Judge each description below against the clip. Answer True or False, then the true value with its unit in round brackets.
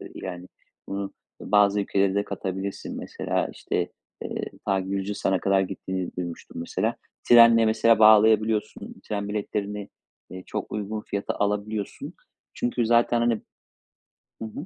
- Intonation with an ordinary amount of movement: False (2.0 semitones)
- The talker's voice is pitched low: True (105 Hz)